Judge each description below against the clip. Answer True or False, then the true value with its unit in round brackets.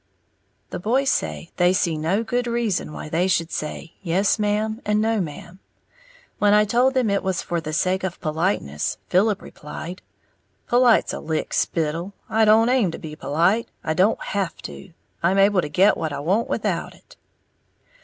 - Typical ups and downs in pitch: True (4.7 semitones)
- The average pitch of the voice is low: False (190 Hz)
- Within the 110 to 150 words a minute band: False (175 wpm)